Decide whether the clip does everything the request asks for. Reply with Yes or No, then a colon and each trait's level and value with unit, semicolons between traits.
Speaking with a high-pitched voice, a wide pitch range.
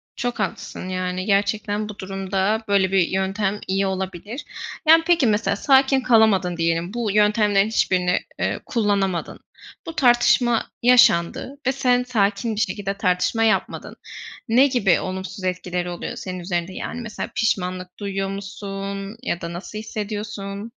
No: high, 200 Hz; average, 3.1 semitones